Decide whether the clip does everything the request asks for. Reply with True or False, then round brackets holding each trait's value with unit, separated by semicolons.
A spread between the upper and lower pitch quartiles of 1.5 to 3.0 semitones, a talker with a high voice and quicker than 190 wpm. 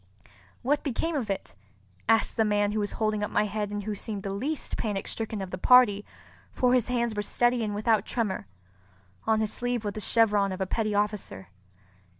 True (2.4 semitones; 215 Hz; 200 wpm)